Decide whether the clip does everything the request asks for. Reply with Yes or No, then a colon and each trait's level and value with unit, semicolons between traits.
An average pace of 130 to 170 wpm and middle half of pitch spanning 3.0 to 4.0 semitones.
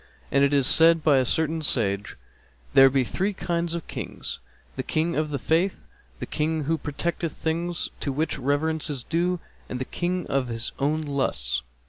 No: average, 180 wpm; average, 3.5 semitones